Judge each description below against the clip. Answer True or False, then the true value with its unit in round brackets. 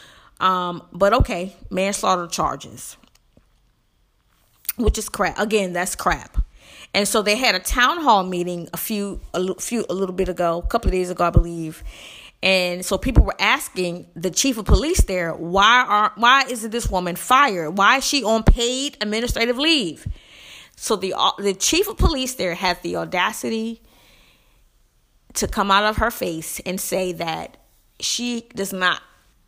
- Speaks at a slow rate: False (165 wpm)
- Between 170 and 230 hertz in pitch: True (190 Hz)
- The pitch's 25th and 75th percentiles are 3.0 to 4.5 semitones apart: True (3.9 semitones)